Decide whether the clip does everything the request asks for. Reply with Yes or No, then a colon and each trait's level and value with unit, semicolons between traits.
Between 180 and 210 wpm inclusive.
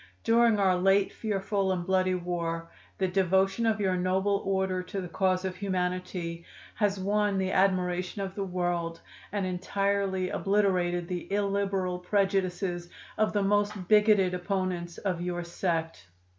No: average, 145 wpm